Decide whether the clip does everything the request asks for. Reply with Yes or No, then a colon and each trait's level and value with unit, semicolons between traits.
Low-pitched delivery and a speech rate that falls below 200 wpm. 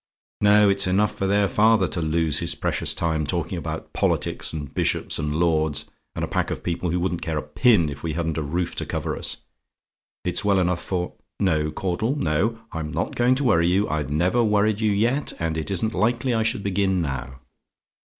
No: very low, 90 Hz; fast, 205 wpm